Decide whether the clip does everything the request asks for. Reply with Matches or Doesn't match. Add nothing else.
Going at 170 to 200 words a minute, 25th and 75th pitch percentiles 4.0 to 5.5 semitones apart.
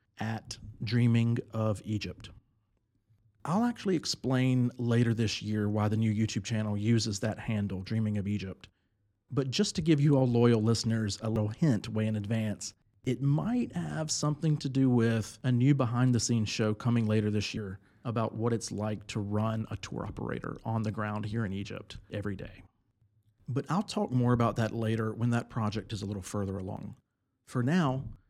Doesn't match